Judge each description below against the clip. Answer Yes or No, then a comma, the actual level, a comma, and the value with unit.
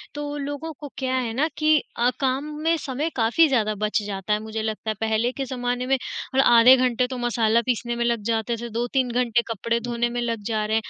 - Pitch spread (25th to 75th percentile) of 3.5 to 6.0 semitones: No, narrow, 2.5 semitones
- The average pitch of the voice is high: Yes, high, 240 Hz